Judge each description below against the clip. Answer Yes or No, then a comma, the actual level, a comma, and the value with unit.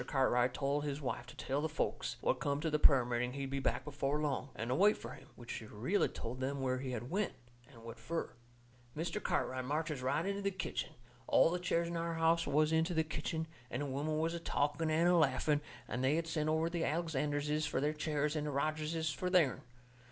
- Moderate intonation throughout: Yes, average, 3.4 semitones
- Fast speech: Yes, fast, 230 wpm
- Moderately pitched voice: Yes, medium, 150 Hz